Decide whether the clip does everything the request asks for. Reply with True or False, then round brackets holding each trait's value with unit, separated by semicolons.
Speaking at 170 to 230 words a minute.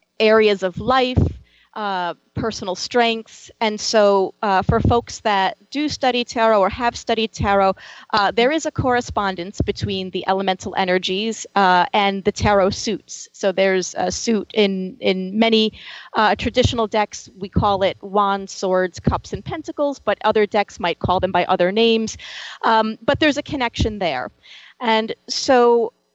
False (155 wpm)